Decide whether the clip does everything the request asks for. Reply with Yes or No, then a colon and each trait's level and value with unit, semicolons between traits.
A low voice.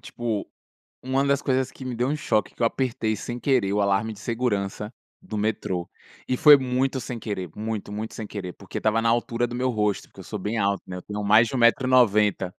Yes: low, 110 Hz